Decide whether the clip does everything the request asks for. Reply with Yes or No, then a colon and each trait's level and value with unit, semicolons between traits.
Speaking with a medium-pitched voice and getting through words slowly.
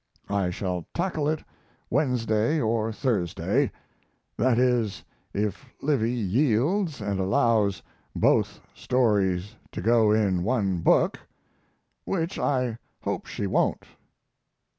No: low, 115 Hz; slow, 105 wpm